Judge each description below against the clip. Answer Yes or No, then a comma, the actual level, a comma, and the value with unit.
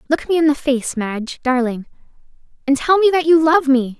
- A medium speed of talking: No, fast, 210 wpm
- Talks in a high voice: Yes, very high, 285 Hz